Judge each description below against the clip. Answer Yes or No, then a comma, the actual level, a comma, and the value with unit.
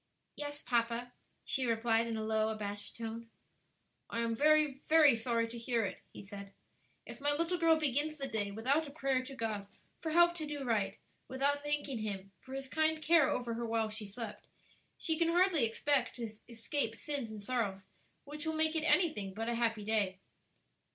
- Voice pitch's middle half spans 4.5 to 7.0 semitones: Yes, average, 4.9 semitones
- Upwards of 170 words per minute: Yes, average, 190 wpm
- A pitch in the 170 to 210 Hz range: No, high, 240 Hz